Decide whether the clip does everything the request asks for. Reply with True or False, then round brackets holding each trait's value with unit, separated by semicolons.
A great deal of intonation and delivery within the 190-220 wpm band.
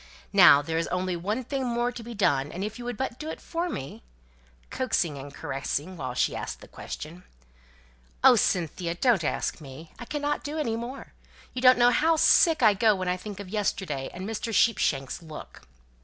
True (7.1 semitones; 200 wpm)